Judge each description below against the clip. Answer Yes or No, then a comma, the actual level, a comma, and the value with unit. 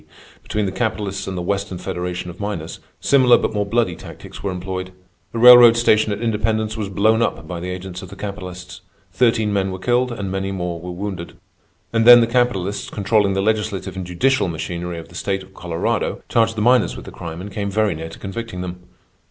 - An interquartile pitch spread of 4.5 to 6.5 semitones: No, average, 3.4 semitones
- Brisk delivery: Yes, fast, 210 wpm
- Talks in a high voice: No, low, 100 Hz